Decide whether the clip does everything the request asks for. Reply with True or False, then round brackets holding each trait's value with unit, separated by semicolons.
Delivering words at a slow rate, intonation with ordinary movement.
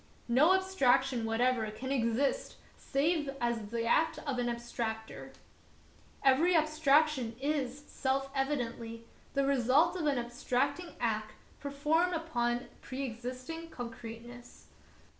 True (110 wpm; 4.1 semitones)